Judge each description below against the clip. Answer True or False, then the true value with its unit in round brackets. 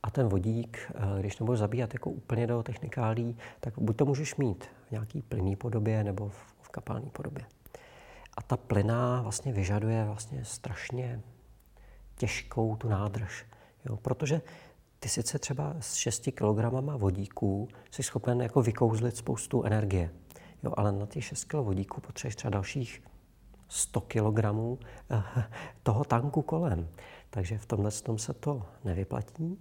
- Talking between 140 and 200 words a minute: True (145 wpm)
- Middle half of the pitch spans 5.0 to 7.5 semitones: False (3.5 semitones)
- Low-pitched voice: True (115 Hz)